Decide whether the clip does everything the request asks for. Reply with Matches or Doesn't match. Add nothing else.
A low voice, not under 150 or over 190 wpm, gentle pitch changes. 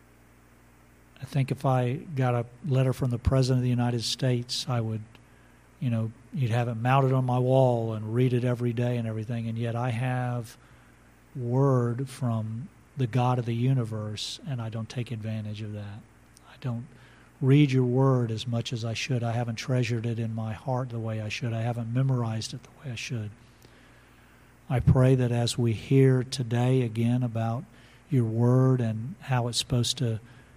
Matches